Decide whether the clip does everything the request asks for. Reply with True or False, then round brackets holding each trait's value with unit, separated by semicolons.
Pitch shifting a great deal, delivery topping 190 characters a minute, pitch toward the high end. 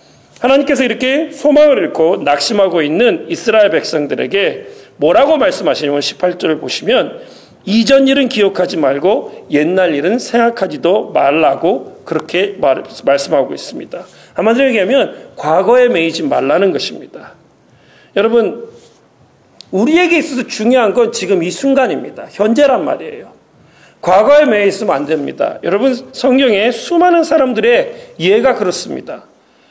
True (6.5 semitones; 320 characters per minute; 255 Hz)